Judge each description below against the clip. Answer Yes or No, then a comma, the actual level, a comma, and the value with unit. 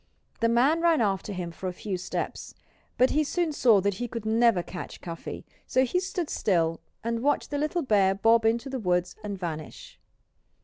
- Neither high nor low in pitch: No, high, 225 Hz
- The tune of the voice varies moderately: No, wide, 6.1 semitones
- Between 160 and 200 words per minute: Yes, average, 190 wpm